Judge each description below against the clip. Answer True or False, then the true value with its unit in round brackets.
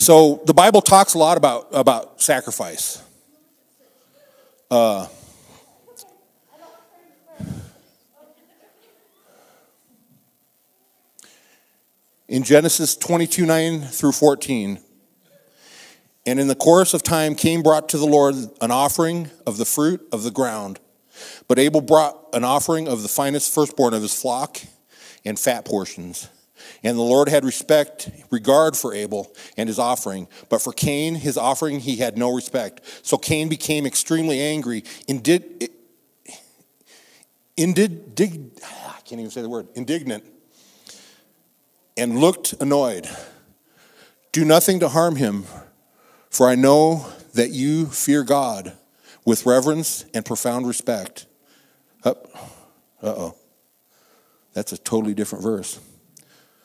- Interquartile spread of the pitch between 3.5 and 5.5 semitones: True (5.1 semitones)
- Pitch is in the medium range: True (150 Hz)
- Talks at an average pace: False (120 wpm)